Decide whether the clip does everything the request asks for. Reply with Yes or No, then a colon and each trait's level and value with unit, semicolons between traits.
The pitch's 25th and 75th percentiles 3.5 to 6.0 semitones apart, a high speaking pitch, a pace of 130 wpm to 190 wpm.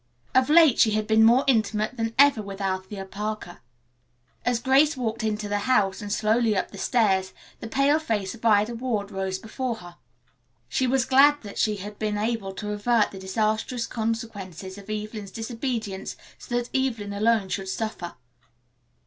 No: average, 3.0 semitones; high, 220 Hz; average, 170 wpm